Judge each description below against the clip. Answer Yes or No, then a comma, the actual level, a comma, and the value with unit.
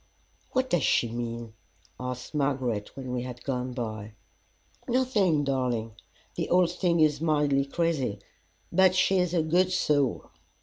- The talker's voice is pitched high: No, medium, 140 Hz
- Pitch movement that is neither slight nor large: No, wide, 5.8 semitones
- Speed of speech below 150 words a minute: Yes, average, 140 wpm